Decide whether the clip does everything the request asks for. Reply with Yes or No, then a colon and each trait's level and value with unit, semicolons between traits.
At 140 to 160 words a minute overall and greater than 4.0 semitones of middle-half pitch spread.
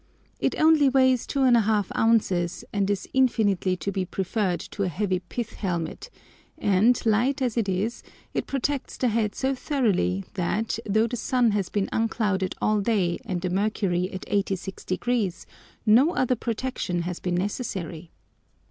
Yes: average, 150 wpm; average, 4.6 semitones